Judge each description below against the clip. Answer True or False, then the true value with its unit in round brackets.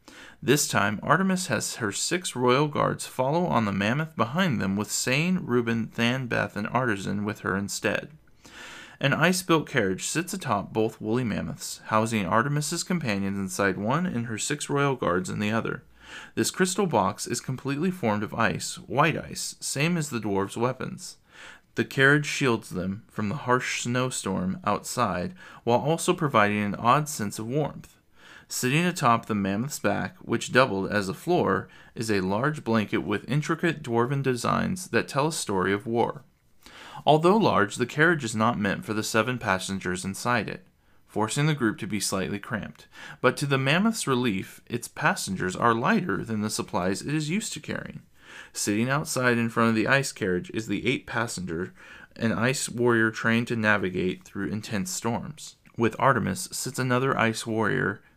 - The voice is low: True (115 Hz)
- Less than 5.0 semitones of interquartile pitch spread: False (5.3 semitones)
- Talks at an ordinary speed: True (170 wpm)